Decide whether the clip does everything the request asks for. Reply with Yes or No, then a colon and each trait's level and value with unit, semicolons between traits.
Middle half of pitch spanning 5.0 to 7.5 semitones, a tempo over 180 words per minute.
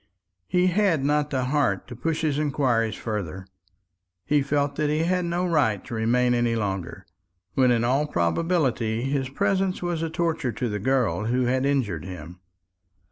No: average, 5.3 semitones; average, 170 wpm